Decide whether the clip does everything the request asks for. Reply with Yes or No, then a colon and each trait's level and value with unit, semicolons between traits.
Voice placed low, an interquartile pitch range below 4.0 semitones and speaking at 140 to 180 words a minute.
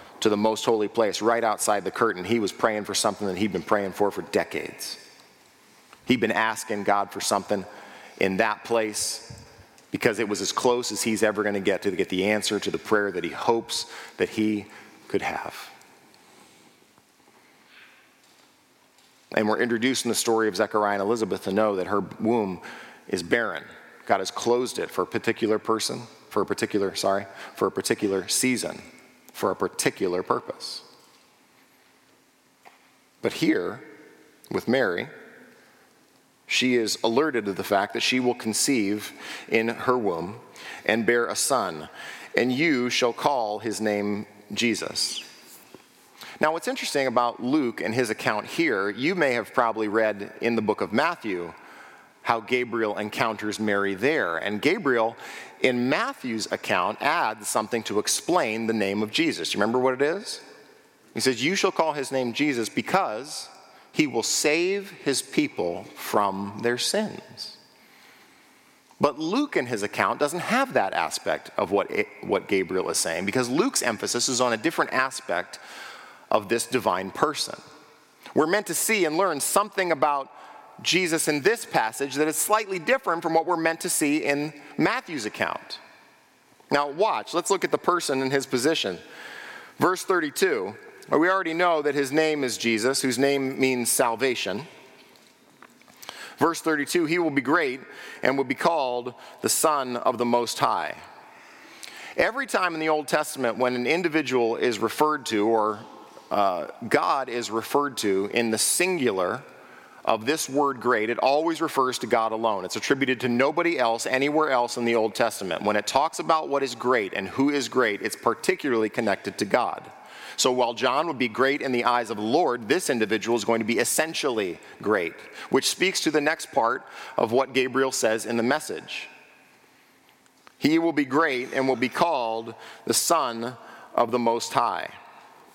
No: low, 125 Hz; average, 5.2 semitones; average, 165 wpm